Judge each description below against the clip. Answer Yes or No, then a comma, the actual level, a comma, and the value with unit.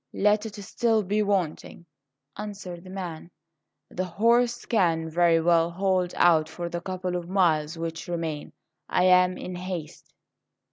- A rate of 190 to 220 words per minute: No, average, 145 wpm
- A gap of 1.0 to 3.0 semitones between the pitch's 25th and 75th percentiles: Yes, average, 2.7 semitones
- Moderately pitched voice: Yes, medium, 180 Hz